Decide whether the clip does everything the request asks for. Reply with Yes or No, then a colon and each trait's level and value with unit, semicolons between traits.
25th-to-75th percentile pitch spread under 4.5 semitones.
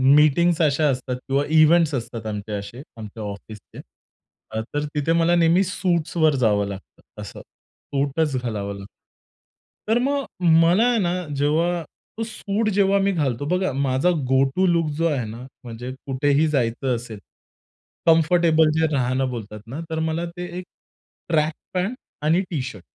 No: wide, 5.5 semitones